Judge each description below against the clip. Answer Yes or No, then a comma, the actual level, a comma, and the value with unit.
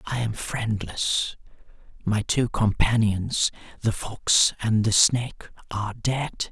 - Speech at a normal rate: No, slow, 120 wpm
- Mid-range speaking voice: No, low, 110 Hz